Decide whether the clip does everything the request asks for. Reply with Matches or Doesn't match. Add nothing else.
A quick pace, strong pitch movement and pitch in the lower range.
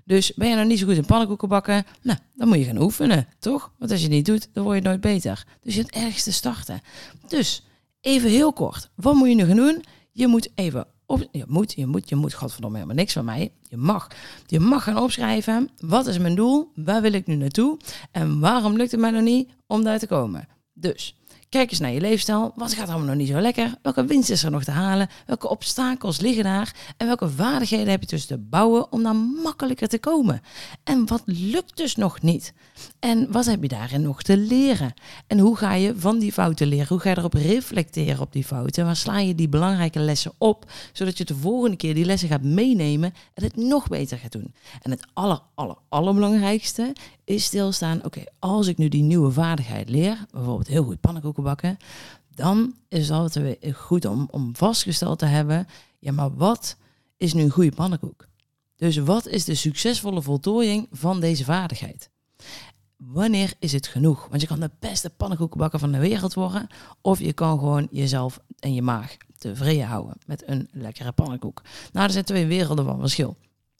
Doesn't match